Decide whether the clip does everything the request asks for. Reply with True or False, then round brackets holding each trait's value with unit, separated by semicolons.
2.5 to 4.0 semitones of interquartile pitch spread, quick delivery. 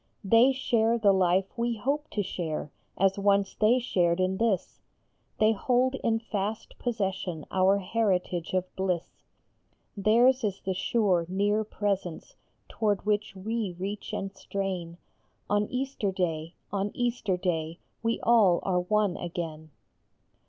False (3.4 semitones; 135 wpm)